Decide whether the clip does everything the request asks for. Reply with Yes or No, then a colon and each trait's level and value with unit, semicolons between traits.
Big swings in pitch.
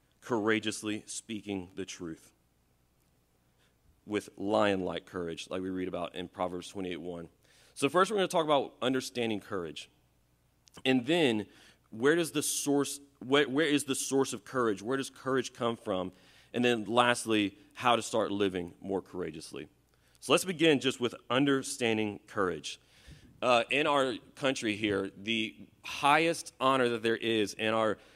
Yes: wide, 6.2 semitones